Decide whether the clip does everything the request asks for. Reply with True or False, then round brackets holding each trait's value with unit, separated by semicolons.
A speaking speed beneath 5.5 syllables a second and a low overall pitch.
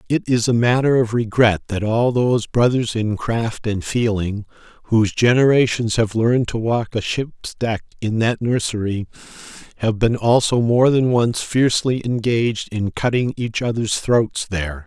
True (4.6 syllables/s; 115 Hz)